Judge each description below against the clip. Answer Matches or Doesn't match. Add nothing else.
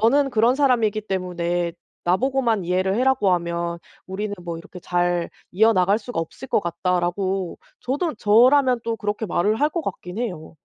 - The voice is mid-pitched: Doesn't match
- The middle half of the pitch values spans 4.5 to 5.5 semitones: Matches